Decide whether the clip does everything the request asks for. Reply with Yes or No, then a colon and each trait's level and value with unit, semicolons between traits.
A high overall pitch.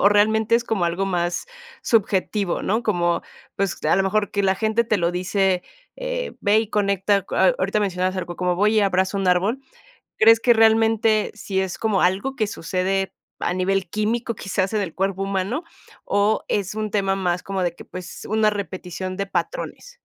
Yes: high, 200 Hz